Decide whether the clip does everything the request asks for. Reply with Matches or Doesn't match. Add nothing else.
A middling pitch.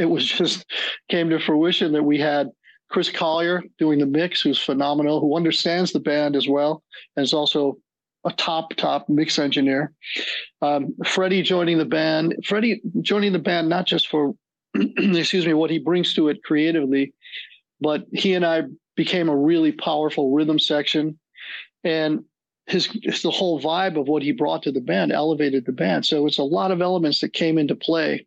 Matches